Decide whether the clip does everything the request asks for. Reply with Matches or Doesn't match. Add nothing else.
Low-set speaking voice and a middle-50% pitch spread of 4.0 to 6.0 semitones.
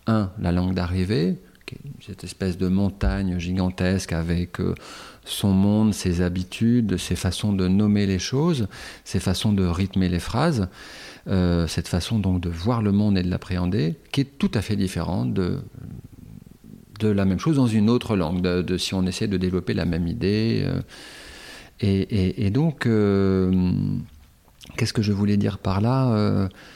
Doesn't match